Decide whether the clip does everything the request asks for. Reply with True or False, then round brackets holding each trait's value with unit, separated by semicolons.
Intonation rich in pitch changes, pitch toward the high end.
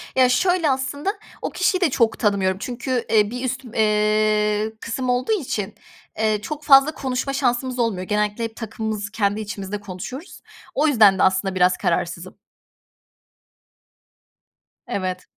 False (4.1 semitones; 220 Hz)